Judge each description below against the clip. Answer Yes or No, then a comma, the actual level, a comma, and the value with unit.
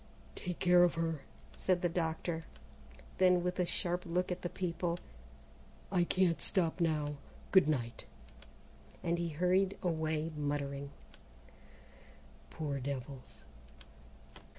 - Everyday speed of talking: No, slow, 110 wpm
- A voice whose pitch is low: No, medium, 170 Hz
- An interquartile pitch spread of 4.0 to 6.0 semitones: No, average, 2.8 semitones